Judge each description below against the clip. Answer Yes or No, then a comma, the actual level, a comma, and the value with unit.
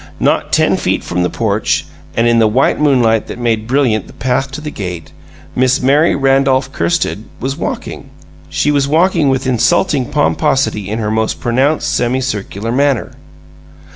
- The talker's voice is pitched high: No, low, 130 Hz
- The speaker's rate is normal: Yes, average, 160 wpm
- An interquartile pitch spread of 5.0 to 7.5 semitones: No, average, 3.8 semitones